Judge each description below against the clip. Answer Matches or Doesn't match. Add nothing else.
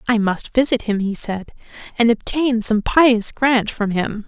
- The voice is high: Matches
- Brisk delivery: Doesn't match